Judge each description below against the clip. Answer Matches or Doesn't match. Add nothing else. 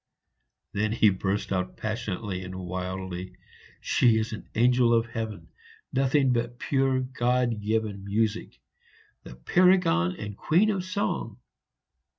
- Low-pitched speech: Matches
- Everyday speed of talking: Doesn't match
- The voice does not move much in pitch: Doesn't match